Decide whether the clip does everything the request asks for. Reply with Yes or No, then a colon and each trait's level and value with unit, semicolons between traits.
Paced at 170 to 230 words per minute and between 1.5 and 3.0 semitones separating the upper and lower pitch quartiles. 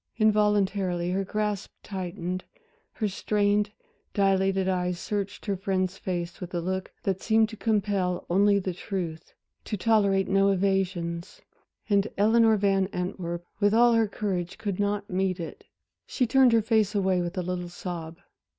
No: average, 150 wpm; narrow, 2.4 semitones